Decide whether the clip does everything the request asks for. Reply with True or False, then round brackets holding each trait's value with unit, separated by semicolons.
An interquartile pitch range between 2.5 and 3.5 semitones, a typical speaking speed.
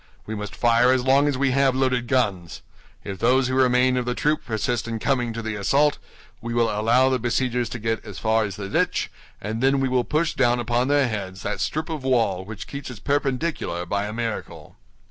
False (3.1 semitones; 220 wpm)